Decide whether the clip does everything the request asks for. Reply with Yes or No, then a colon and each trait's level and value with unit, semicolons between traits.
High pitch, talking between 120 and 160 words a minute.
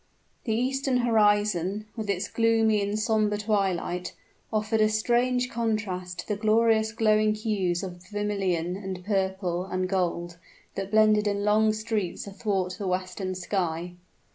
Yes: high, 205 Hz; average, 140 wpm